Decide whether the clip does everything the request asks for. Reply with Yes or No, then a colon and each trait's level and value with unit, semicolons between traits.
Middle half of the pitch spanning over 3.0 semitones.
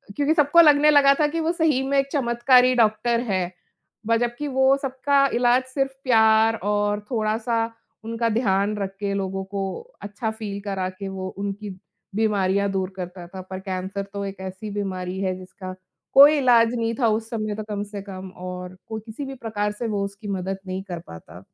Yes: average, 4.0 semitones